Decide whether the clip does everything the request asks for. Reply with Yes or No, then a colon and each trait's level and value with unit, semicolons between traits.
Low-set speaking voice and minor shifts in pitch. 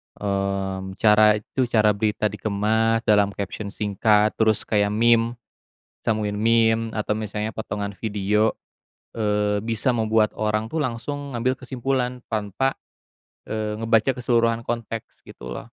Yes: low, 110 Hz; narrow, 1.9 semitones